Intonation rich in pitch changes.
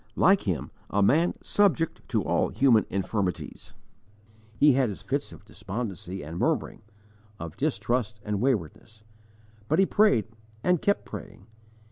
Yes: wide, 7.4 semitones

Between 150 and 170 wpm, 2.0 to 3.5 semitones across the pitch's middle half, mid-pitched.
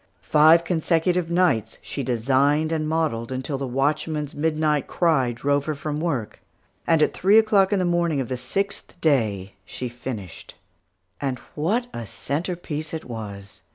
No: average, 155 wpm; average, 4.4 semitones; medium, 150 Hz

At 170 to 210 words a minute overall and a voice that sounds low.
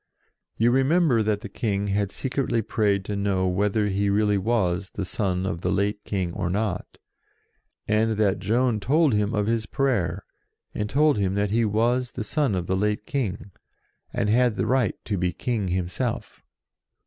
Yes: average, 180 wpm; low, 105 Hz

